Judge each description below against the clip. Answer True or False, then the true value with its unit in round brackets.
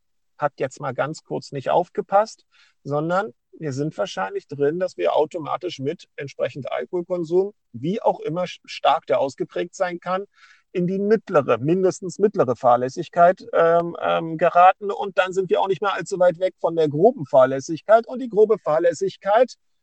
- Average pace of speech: True (160 wpm)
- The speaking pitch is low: False (180 Hz)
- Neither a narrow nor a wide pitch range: True (3.7 semitones)